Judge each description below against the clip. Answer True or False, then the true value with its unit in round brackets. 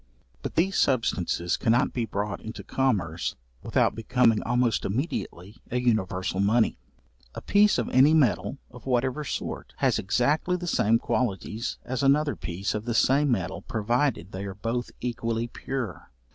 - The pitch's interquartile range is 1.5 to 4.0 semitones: False (4.4 semitones)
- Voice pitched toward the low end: True (115 Hz)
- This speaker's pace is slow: False (150 wpm)